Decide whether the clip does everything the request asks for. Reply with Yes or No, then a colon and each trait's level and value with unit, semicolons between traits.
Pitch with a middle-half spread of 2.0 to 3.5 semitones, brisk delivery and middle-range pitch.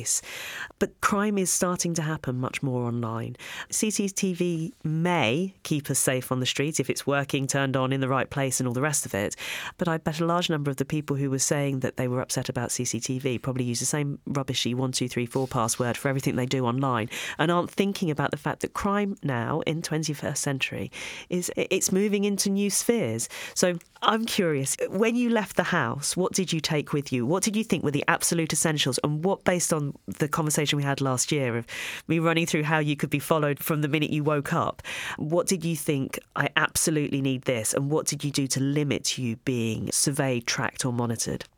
No: average, 4.4 semitones; fast, 220 wpm; medium, 145 Hz